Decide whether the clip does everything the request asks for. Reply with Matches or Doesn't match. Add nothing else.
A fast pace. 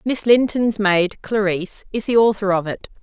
Doesn't match